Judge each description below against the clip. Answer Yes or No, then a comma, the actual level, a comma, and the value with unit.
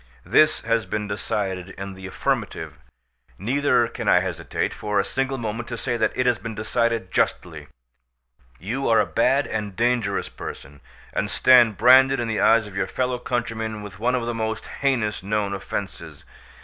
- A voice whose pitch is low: Yes, low, 115 Hz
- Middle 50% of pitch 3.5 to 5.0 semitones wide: No, average, 3.1 semitones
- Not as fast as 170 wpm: No, average, 175 wpm